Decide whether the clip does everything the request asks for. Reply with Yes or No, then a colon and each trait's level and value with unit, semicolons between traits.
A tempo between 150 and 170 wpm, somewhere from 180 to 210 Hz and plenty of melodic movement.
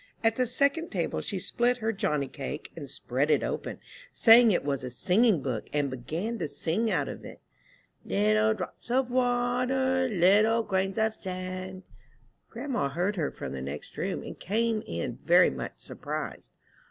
Yes: average, 165 wpm; high, 190 Hz; wide, 8.5 semitones